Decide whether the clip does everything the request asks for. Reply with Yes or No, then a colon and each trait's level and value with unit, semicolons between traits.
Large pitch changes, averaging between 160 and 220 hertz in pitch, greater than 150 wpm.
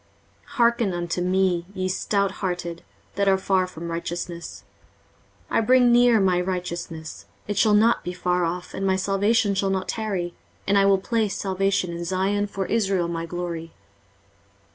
No: narrow, 2.4 semitones; high, 190 Hz; average, 165 wpm